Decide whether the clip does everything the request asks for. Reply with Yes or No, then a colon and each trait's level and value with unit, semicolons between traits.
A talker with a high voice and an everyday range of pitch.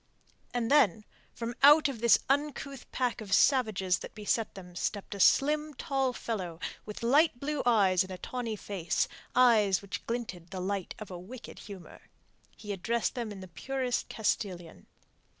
Yes: high, 220 Hz; average, 5.0 semitones